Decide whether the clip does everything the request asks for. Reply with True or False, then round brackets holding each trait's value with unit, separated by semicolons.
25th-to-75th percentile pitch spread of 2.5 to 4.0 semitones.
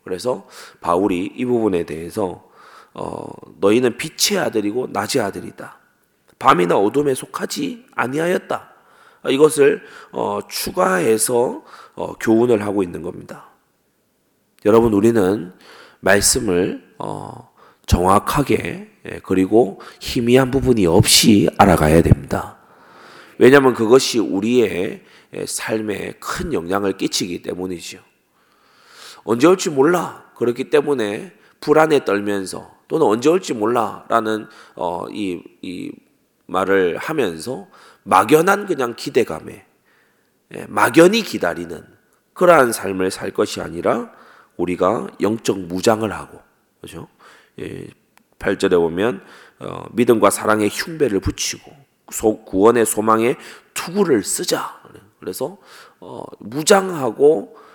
False (5.3 semitones)